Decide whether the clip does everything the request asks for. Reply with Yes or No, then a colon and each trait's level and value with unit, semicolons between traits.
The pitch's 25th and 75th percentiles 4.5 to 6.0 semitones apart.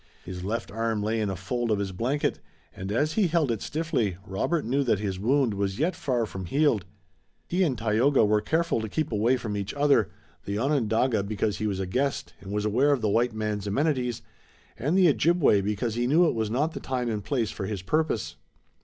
Yes: average, 5.3 semitones